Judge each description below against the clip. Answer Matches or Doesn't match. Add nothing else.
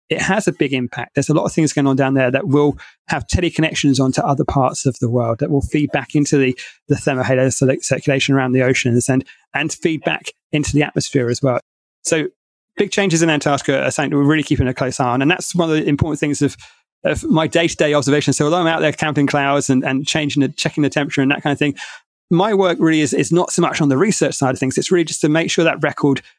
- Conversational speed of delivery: Doesn't match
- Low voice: Doesn't match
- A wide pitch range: Doesn't match